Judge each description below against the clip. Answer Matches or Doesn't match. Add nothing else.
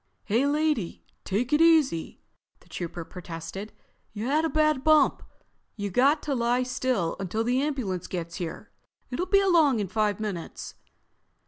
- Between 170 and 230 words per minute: Doesn't match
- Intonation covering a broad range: Matches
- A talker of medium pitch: Doesn't match